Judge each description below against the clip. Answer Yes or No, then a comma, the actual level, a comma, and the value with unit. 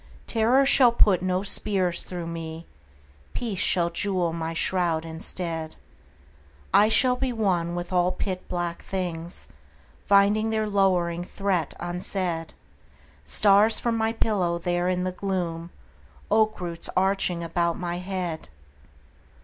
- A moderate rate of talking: No, slow, 125 wpm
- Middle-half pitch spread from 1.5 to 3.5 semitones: Yes, average, 2.9 semitones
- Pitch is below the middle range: No, medium, 180 Hz